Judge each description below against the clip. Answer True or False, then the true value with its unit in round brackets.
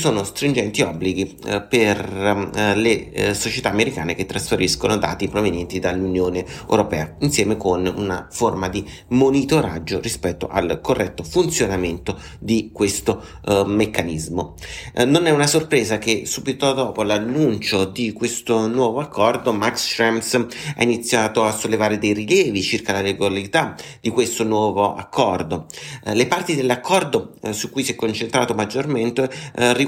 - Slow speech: False (140 wpm)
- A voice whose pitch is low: True (105 Hz)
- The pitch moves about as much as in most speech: True (4.0 semitones)